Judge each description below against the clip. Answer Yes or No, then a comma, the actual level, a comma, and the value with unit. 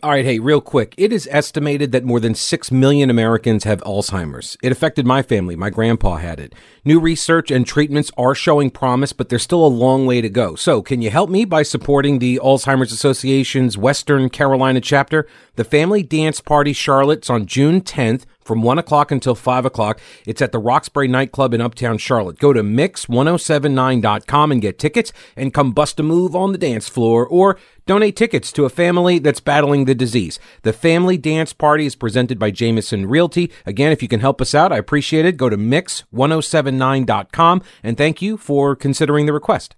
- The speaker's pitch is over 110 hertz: Yes, low, 135 Hz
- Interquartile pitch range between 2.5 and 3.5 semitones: No, average, 4.1 semitones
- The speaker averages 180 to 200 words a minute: Yes, average, 195 wpm